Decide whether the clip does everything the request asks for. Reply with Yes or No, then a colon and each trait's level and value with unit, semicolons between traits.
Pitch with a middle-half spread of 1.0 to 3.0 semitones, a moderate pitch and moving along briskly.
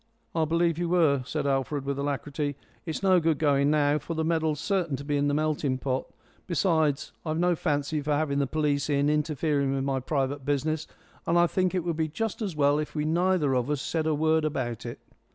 Yes: narrow, 2.4 semitones; medium, 150 Hz; fast, 220 wpm